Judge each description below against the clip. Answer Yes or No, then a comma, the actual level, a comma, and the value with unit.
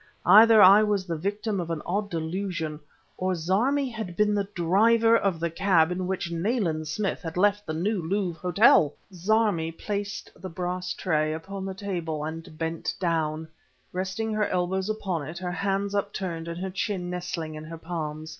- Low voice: No, medium, 185 Hz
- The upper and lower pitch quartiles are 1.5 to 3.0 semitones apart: No, average, 3.6 semitones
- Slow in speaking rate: No, average, 175 wpm